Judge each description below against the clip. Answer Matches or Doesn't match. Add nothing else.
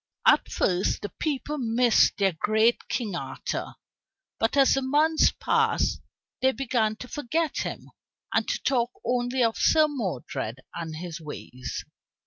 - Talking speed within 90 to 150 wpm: Matches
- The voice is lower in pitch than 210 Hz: Doesn't match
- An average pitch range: Doesn't match